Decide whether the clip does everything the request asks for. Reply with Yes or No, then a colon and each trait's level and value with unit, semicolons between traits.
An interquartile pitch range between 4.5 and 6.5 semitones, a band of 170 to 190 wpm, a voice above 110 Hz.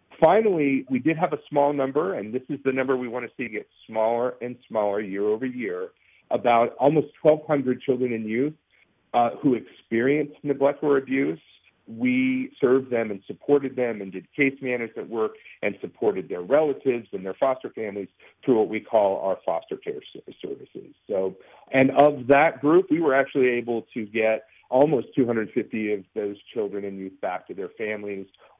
Yes: average, 4.9 semitones; average, 175 wpm; low, 135 Hz